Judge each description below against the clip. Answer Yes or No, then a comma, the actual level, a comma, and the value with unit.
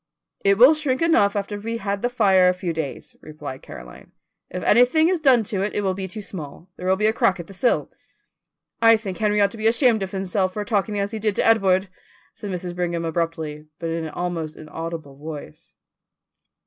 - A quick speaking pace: Yes, fast, 215 wpm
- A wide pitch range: No, average, 4.4 semitones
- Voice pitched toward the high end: Yes, high, 195 Hz